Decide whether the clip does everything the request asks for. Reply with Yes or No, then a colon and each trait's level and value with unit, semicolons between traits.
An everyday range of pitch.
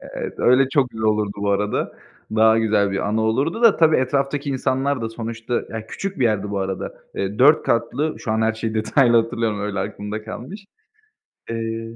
Yes: average, 3.7 semitones